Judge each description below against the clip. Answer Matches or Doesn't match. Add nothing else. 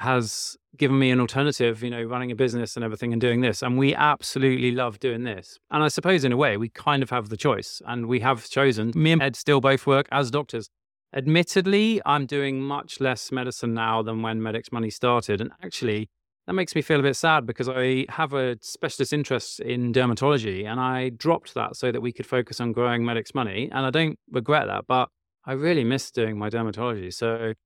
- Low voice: Matches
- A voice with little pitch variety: Doesn't match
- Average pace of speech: Doesn't match